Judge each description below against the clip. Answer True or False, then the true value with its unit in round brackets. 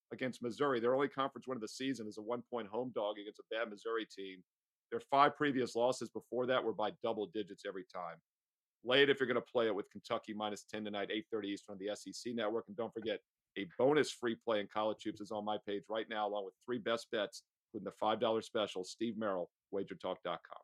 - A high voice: False (110 Hz)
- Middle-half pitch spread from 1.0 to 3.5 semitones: True (2.6 semitones)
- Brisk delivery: True (230 wpm)